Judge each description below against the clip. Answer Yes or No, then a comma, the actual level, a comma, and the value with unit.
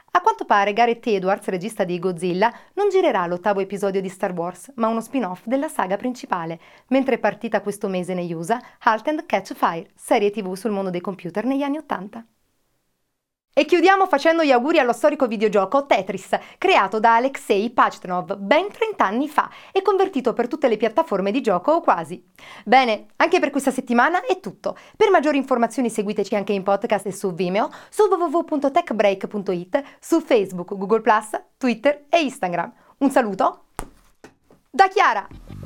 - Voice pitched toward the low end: No, high, 235 Hz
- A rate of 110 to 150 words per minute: No, average, 165 wpm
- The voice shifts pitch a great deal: Yes, wide, 6.5 semitones